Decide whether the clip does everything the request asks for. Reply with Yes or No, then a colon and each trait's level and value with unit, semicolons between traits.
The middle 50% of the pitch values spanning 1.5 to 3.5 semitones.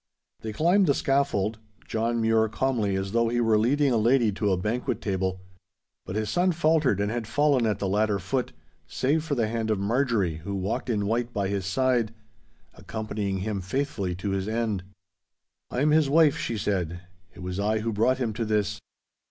No: average, 4.2 semitones